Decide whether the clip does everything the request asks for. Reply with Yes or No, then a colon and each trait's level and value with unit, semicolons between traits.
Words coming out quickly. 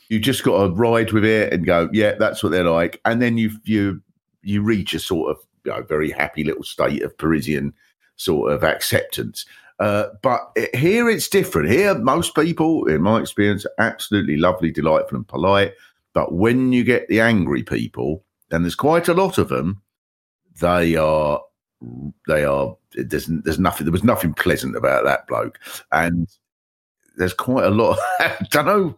No: average, 185 wpm